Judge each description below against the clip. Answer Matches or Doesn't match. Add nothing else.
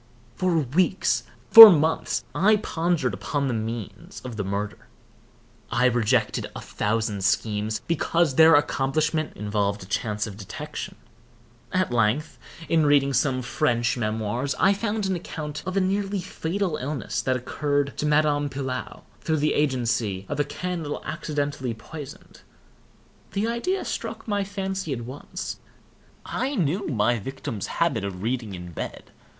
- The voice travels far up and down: Matches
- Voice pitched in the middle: Matches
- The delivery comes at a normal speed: Matches